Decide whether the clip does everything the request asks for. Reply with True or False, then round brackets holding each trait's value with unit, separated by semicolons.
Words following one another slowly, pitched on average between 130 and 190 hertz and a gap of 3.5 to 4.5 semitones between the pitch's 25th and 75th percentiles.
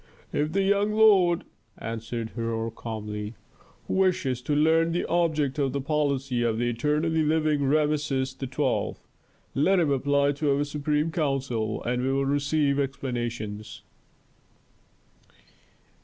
True (125 wpm; 140 Hz; 4.0 semitones)